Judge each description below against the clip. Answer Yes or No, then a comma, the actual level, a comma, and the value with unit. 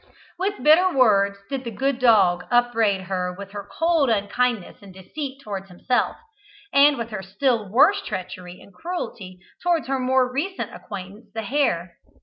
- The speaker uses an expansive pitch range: Yes, wide, 6.0 semitones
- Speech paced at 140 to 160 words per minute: Yes, average, 155 wpm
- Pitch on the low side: No, high, 230 Hz